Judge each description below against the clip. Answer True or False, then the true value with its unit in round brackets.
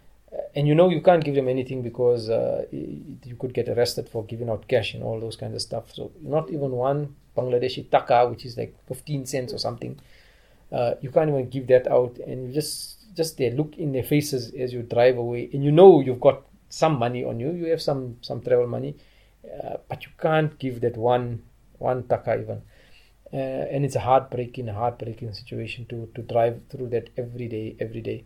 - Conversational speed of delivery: False (210 wpm)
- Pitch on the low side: True (125 Hz)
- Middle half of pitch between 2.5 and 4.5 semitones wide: True (3.2 semitones)